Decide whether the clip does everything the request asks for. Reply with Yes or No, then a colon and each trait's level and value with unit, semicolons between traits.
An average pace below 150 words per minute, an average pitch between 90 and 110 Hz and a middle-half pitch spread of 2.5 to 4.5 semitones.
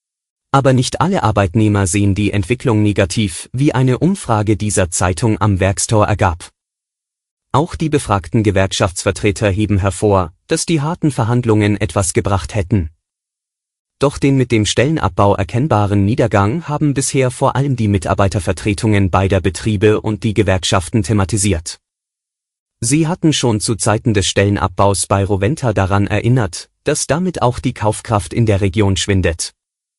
Yes: average, 135 wpm; low, 105 Hz; average, 3.6 semitones